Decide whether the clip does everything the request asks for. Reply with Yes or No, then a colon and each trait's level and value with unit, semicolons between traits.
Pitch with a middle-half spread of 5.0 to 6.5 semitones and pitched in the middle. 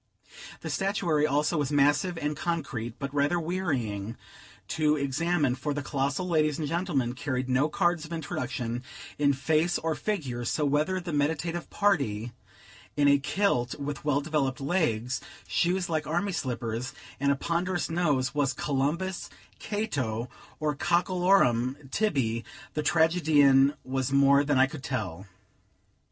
No: average, 4.1 semitones; medium, 145 Hz